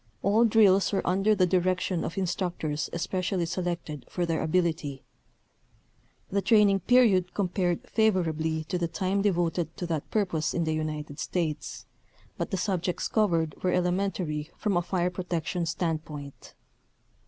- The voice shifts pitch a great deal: No, average, 2.9 semitones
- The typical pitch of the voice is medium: Yes, medium, 180 Hz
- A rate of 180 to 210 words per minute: No, average, 145 wpm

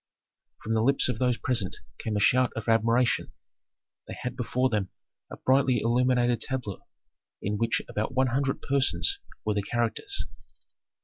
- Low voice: Yes, low, 120 Hz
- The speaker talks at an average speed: Yes, average, 150 wpm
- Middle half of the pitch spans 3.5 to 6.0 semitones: No, narrow, 2.6 semitones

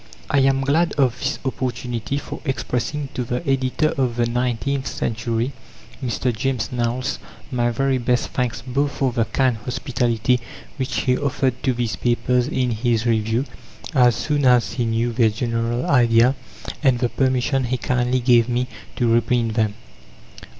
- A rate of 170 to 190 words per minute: No, average, 155 wpm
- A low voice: Yes, low, 125 Hz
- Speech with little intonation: Yes, narrow, 2.1 semitones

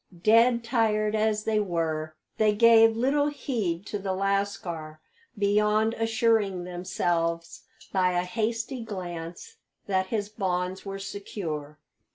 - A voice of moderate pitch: No, high, 200 Hz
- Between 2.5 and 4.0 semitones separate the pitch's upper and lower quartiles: Yes, average, 3.7 semitones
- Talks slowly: Yes, slow, 120 wpm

